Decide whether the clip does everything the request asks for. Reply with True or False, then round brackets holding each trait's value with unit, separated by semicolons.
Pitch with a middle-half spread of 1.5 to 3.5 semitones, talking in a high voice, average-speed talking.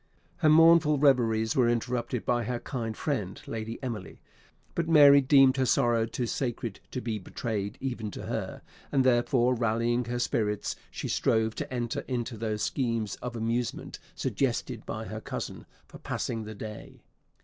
False (2.6 semitones; 120 Hz; 160 wpm)